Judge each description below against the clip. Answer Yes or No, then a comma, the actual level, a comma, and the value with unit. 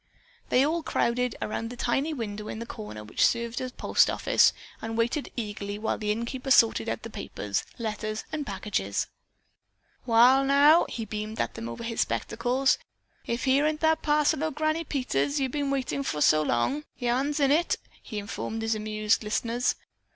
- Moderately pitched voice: No, high, 235 Hz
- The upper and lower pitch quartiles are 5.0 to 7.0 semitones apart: No, average, 4.6 semitones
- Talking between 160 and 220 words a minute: Yes, average, 170 wpm